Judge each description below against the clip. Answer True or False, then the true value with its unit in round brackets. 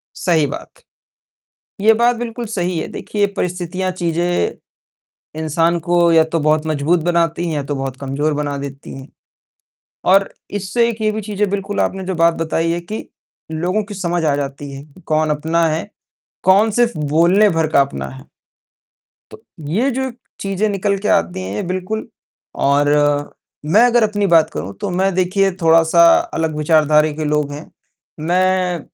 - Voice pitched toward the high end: False (170 Hz)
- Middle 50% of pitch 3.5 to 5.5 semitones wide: True (4.3 semitones)